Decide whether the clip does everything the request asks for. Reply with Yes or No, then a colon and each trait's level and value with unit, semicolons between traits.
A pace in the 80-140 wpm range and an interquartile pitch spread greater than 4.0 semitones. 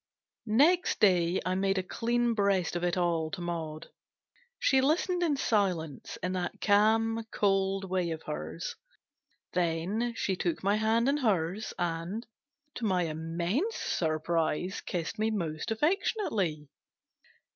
Yes: slow, 135 wpm; average, 4.8 semitones